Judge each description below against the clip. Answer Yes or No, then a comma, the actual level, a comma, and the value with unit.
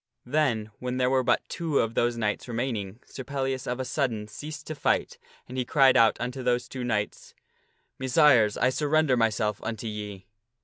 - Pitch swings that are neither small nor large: Yes, average, 3.1 semitones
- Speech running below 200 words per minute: Yes, average, 185 wpm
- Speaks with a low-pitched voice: Yes, low, 125 Hz